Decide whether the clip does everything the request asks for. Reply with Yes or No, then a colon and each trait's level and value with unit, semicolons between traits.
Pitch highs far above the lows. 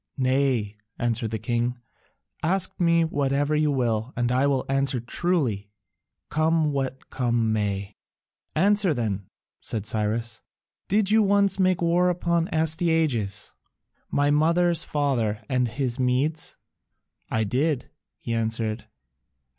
Yes: wide, 5.9 semitones